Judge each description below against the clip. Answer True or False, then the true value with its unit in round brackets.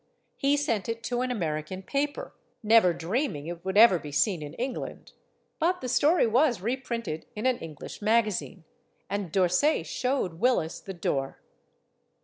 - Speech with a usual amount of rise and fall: False (6.8 semitones)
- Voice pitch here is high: True (215 Hz)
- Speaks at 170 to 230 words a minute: False (150 wpm)